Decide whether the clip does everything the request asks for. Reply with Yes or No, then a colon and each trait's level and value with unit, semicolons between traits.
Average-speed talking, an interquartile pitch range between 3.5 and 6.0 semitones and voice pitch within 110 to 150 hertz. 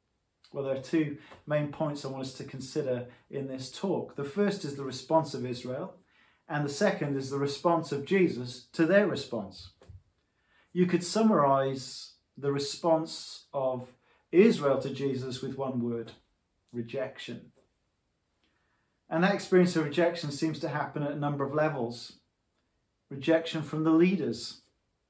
Yes: average, 150 wpm; average, 4.2 semitones; medium, 140 Hz